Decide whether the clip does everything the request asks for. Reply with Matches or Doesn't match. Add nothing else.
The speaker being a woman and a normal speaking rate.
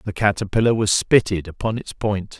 Doesn't match